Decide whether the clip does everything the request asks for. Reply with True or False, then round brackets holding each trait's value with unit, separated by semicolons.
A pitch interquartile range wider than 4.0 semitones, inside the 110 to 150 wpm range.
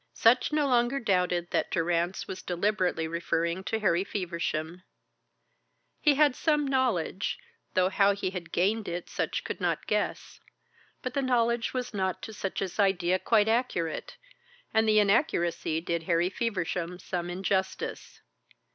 True (4.8 semitones; 140 wpm)